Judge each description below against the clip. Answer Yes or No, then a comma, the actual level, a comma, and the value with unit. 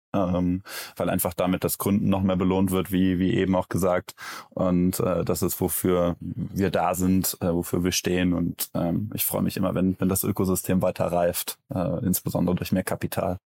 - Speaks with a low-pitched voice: Yes, very low, 90 Hz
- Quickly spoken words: Yes, fast, 195 wpm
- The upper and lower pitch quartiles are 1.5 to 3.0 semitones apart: No, narrow, 0.9 semitones